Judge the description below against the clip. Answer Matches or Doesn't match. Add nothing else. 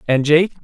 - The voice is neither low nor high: Matches